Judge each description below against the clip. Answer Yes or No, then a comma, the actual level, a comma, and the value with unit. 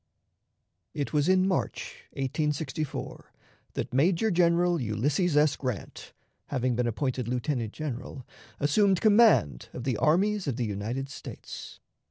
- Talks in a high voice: No, medium, 145 Hz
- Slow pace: Yes, slow, 125 wpm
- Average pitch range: No, wide, 5.7 semitones